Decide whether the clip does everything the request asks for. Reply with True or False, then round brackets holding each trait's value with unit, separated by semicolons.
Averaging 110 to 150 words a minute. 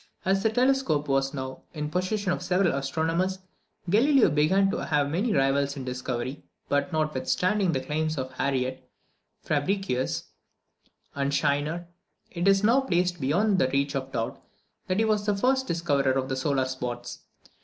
False (160 wpm)